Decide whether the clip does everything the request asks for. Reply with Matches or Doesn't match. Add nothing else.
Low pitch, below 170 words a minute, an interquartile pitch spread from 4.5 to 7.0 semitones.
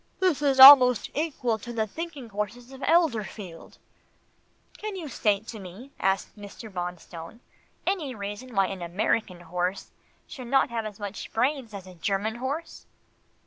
Doesn't match